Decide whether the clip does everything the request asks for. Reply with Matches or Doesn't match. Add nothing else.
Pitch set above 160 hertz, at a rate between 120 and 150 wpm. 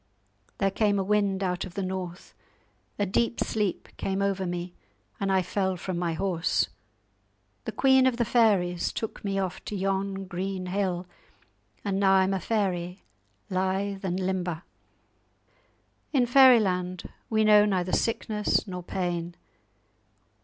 Matches